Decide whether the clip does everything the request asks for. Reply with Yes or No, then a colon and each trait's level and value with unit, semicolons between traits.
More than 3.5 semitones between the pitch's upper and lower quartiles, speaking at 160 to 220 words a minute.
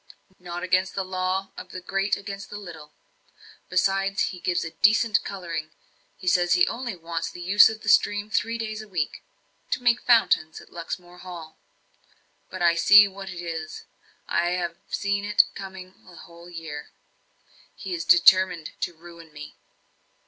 No: average, 2.7 semitones; average, 165 wpm